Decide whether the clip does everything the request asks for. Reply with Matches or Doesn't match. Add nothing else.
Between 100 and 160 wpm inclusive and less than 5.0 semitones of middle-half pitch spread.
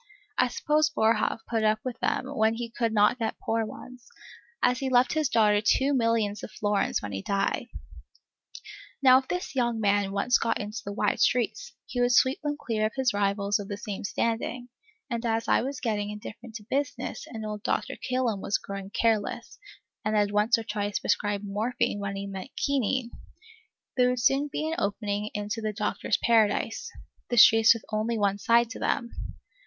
Doesn't match